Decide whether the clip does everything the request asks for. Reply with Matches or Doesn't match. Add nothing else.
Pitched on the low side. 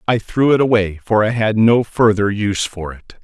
Matches